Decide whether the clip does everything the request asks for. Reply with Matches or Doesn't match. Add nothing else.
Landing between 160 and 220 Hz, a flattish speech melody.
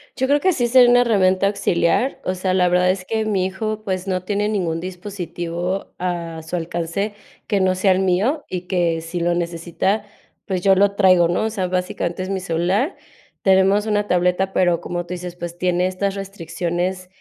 Matches